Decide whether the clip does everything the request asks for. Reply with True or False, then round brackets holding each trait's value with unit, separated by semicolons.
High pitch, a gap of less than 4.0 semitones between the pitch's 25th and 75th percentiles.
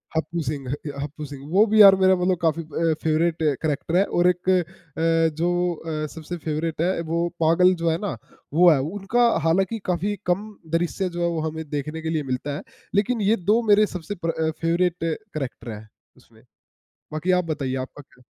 False (165 Hz; 3.0 semitones)